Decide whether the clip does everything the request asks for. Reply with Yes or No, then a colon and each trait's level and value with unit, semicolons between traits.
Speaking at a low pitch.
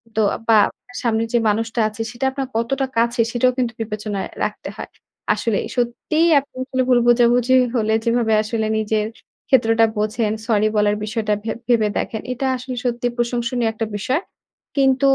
No: high, 235 Hz